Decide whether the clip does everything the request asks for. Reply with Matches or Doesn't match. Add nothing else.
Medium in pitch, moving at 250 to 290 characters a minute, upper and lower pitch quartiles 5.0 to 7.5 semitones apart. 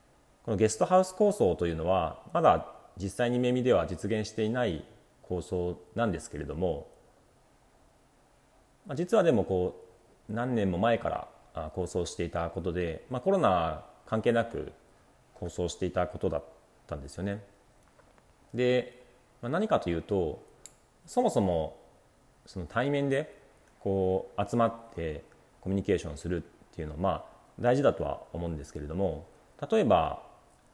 Doesn't match